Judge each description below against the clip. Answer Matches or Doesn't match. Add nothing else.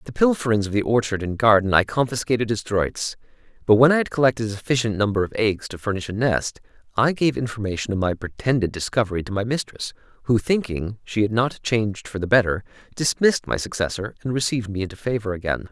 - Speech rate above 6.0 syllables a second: Matches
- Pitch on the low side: Matches